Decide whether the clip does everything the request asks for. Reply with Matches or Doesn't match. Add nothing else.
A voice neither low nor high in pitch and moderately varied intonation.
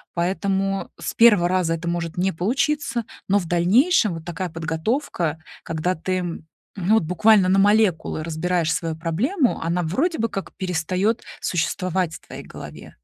Matches